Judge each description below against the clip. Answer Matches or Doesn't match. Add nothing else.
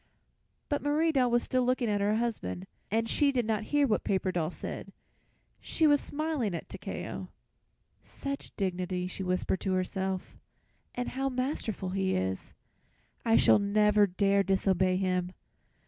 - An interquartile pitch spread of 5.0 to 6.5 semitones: Matches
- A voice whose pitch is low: Doesn't match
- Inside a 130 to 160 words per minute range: Matches